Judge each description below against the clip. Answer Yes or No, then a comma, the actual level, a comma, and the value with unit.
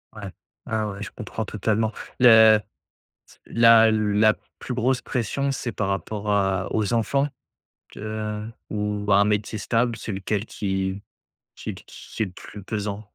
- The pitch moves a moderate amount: No, narrow, 1.7 semitones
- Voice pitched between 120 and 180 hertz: No, low, 105 Hz